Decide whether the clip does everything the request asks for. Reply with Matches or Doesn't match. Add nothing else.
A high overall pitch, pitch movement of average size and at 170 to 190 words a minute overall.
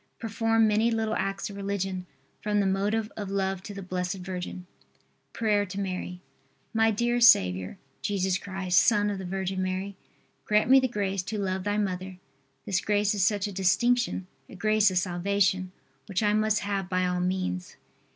Doesn't match